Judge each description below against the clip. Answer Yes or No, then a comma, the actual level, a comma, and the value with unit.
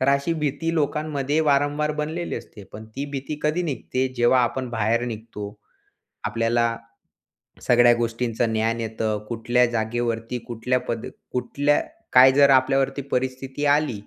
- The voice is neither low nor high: No, low, 125 Hz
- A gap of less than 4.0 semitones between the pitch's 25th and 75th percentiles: Yes, average, 3.6 semitones